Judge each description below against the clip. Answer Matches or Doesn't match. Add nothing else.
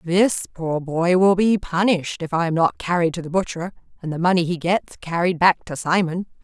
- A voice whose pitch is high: Doesn't match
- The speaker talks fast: Matches